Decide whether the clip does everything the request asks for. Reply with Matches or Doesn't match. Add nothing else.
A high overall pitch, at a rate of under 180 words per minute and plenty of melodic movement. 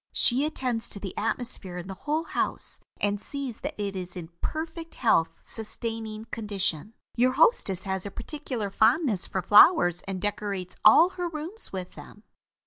Matches